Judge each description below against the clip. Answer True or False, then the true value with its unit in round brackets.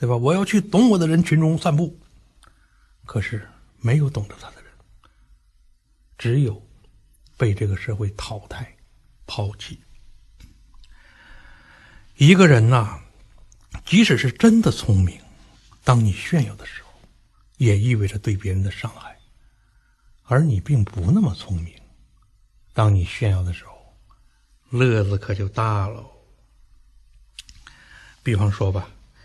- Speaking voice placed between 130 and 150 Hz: False (110 Hz)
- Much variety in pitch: False (4.7 semitones)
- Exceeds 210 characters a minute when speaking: False (175 characters per minute)